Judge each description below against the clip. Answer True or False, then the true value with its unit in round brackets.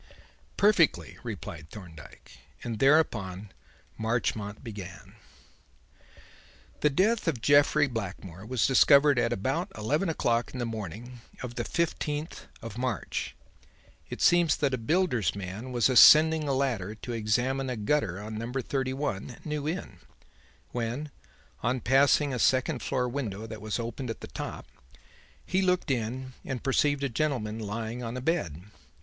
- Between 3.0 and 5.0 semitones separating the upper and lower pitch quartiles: True (4.7 semitones)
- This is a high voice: False (125 Hz)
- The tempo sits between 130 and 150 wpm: True (145 wpm)